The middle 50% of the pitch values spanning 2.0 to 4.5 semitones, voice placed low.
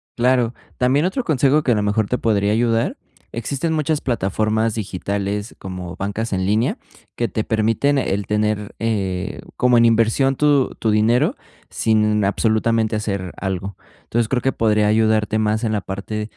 Yes: narrow, 2.6 semitones; low, 110 Hz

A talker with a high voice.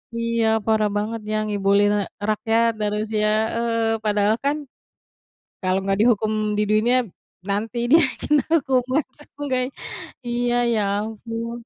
Yes: high, 225 Hz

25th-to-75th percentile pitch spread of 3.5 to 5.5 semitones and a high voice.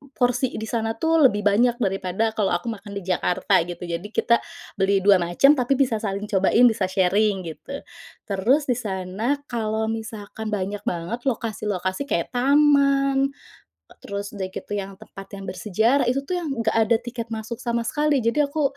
Yes: average, 4.2 semitones; high, 220 Hz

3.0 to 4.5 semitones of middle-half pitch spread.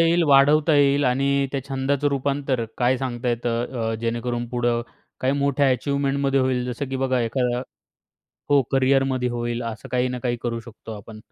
No: narrow, 2.4 semitones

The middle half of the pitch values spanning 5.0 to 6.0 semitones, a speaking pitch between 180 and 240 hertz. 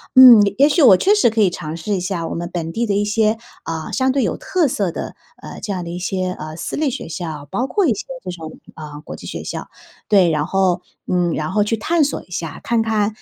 Yes: average, 5.3 semitones; high, 195 Hz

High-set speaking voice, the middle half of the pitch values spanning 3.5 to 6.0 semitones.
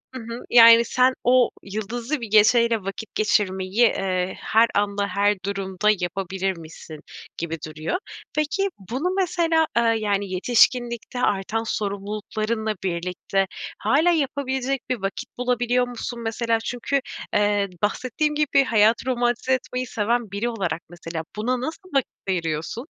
Yes: high, 225 Hz; average, 4.1 semitones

